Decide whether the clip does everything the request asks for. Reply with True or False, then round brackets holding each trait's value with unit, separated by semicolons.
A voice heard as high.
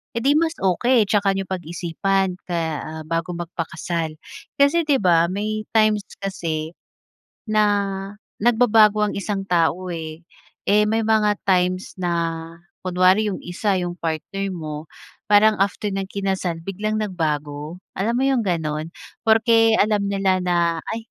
True (195 Hz)